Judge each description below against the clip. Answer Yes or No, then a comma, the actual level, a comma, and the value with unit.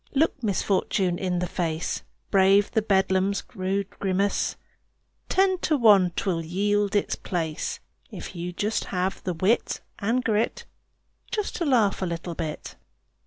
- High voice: Yes, high, 195 Hz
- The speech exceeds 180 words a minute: No, slow, 135 wpm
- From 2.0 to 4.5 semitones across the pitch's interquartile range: Yes, average, 2.8 semitones